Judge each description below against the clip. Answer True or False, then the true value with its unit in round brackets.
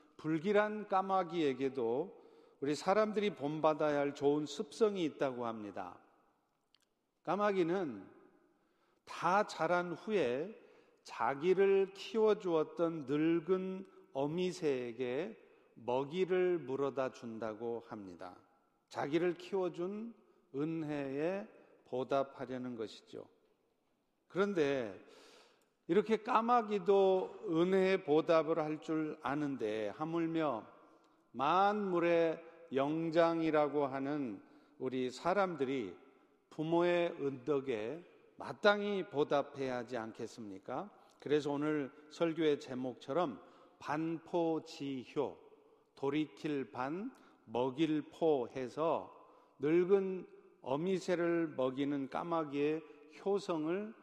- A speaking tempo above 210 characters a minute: False (205 characters per minute)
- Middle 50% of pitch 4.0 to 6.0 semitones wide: True (5.3 semitones)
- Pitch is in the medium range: True (160 Hz)